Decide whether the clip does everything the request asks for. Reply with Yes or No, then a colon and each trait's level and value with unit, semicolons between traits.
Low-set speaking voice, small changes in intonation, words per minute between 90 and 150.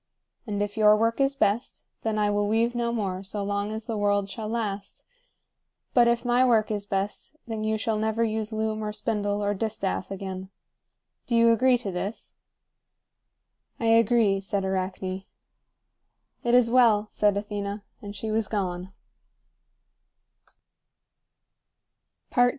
No: high, 215 Hz; narrow, 2.1 semitones; average, 145 wpm